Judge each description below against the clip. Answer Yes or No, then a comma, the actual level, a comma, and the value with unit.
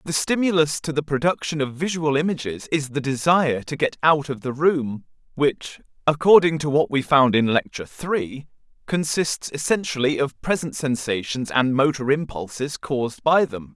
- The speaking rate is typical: Yes, average, 160 wpm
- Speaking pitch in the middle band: Yes, medium, 145 Hz